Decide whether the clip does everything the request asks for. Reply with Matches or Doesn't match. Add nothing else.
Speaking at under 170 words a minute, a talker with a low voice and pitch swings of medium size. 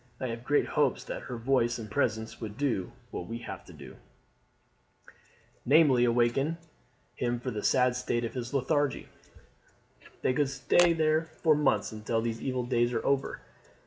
Matches